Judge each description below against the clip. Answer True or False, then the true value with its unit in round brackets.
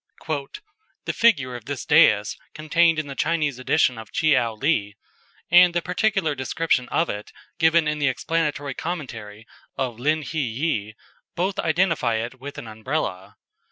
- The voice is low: False (145 Hz)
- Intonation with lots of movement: True (5.8 semitones)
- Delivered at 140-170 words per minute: True (150 wpm)